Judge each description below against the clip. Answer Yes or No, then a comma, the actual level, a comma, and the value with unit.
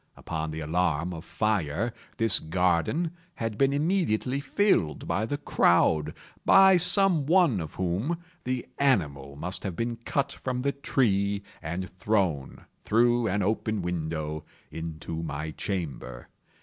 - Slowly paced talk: Yes, slow, 130 wpm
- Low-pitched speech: Yes, low, 100 Hz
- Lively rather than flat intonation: Yes, wide, 7.9 semitones